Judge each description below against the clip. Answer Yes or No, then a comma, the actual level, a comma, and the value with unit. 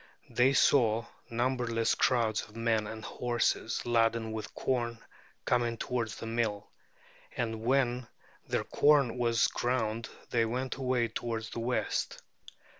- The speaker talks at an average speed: No, slow, 125 wpm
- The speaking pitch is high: No, low, 115 Hz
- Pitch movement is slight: Yes, narrow, 1.7 semitones